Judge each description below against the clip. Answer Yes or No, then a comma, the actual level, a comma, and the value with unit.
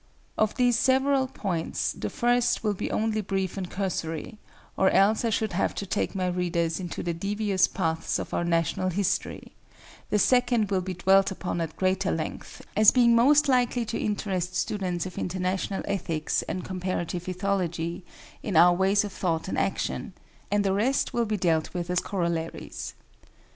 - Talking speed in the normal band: Yes, average, 170 wpm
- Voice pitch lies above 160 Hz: Yes, high, 190 Hz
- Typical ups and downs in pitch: Yes, average, 3.4 semitones